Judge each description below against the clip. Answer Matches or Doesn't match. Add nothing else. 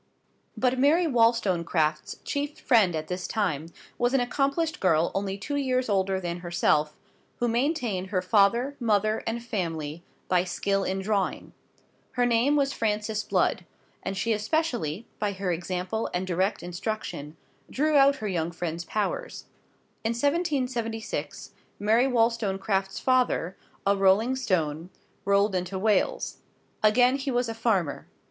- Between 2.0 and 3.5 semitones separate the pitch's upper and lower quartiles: Doesn't match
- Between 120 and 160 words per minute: Matches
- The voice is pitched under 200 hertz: Doesn't match